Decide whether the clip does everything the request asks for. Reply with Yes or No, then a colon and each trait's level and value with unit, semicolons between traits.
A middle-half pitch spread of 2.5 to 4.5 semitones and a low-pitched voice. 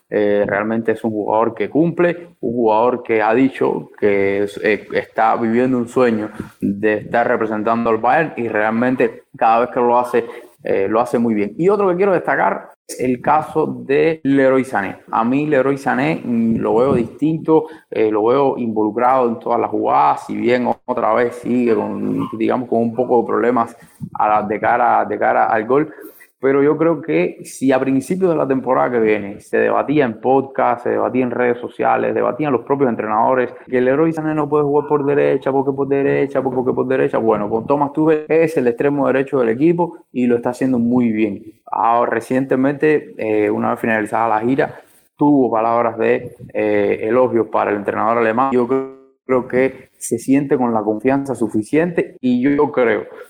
Yes: average, 4.1 semitones; low, 125 Hz